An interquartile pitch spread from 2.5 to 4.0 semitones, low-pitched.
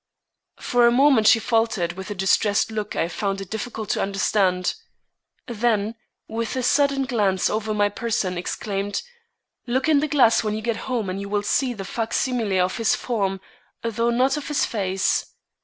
No: average, 3.3 semitones; high, 220 Hz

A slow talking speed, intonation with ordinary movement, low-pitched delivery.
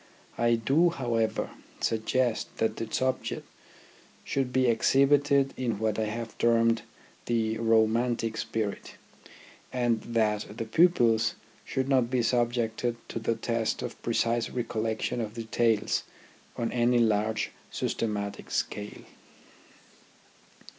No: slow, 115 wpm; narrow, 1.8 semitones; low, 115 Hz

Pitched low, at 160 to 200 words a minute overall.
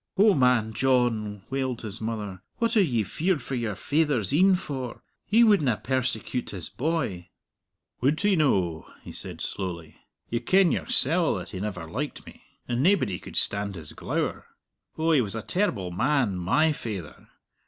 Yes: low, 125 Hz; average, 165 wpm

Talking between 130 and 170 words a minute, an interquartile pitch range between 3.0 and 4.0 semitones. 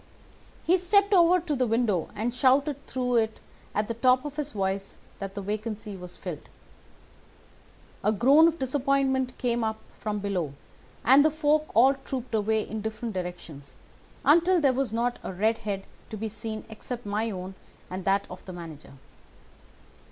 No: average, 165 wpm; average, 5.2 semitones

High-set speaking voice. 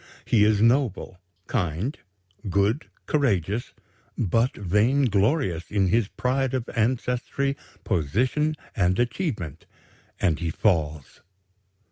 No: low, 110 Hz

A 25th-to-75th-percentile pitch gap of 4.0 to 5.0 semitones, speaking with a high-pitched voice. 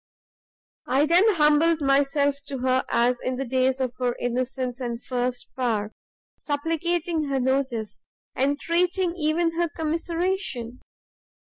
Yes: average, 4.5 semitones; very high, 275 Hz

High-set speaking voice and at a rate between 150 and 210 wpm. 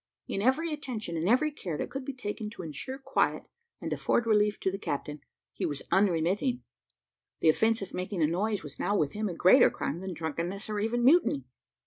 Yes: high, 205 Hz; average, 200 wpm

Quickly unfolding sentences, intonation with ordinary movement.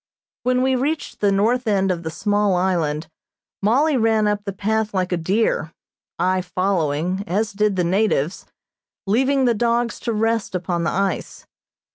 No: average, 160 wpm; average, 3.7 semitones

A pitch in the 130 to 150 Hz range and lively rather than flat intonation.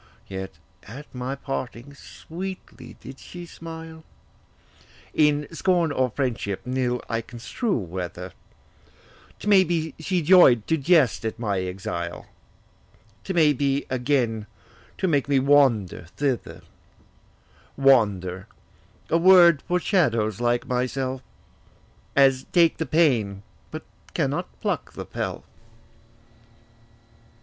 Yes: low, 135 Hz; wide, 6.2 semitones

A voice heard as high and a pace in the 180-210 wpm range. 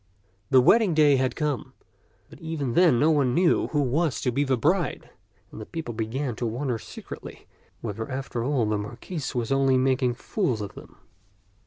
No: low, 130 Hz; average, 185 wpm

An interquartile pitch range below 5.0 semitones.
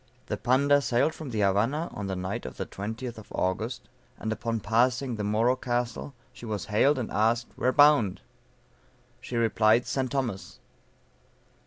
Yes: average, 3.4 semitones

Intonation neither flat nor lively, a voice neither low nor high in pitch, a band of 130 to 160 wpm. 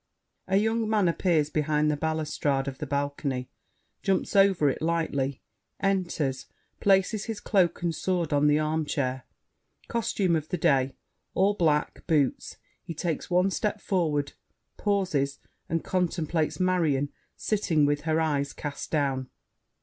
Yes: average, 4.3 semitones; medium, 160 Hz; slow, 135 wpm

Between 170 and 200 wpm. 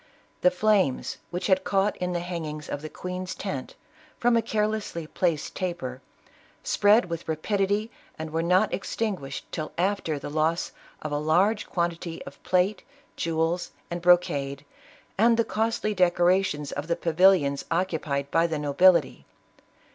No: average, 145 wpm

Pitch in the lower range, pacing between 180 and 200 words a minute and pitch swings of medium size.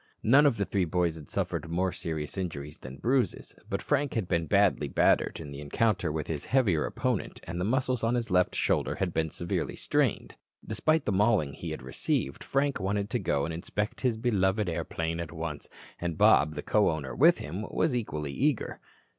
No: very low, 90 Hz; average, 195 wpm; wide, 6.3 semitones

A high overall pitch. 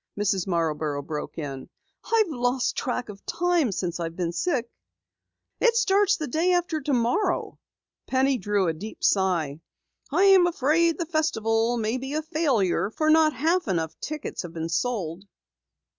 Yes: high, 245 Hz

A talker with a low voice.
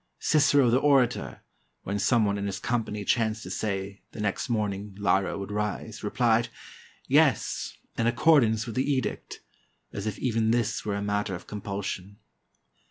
Yes: low, 105 Hz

